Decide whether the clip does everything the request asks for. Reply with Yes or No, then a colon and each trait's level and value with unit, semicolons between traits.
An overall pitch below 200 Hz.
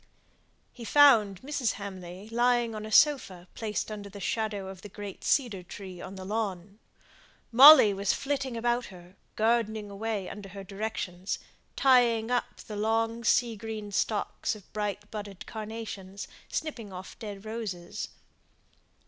No: high, 215 Hz